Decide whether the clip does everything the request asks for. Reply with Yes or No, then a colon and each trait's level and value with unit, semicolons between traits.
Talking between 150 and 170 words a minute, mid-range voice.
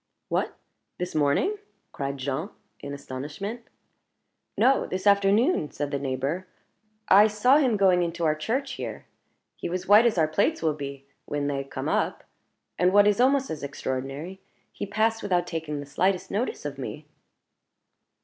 Yes: average, 160 wpm; medium, 180 Hz